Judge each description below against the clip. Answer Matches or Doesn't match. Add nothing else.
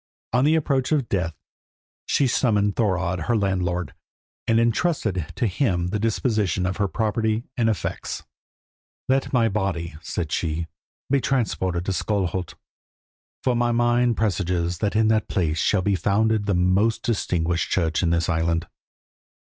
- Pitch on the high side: Doesn't match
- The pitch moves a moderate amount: Matches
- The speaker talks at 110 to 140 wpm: Doesn't match